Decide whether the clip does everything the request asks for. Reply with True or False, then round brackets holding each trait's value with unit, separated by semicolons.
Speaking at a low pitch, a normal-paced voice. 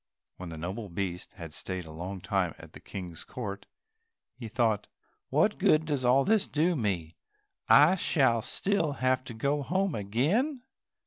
True (115 Hz; 165 wpm)